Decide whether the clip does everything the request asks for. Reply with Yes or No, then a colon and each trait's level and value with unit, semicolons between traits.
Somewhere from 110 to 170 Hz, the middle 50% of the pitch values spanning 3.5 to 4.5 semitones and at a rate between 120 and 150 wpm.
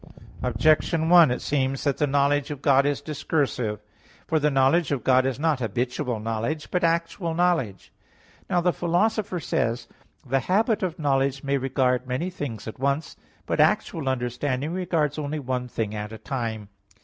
No: medium, 140 Hz; average, 4.2 semitones; average, 175 wpm